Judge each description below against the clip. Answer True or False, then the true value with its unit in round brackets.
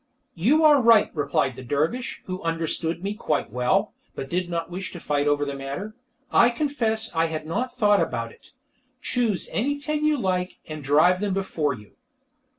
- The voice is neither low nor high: True (180 Hz)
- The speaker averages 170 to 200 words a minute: True (175 wpm)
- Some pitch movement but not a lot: False (7.2 semitones)